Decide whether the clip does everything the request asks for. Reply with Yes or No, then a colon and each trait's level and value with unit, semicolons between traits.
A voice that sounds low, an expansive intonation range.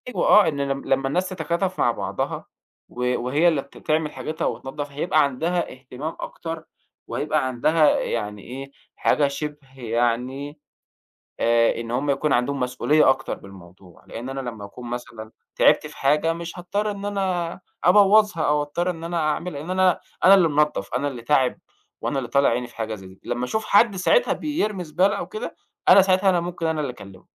No: medium, 145 Hz; wide, 5.8 semitones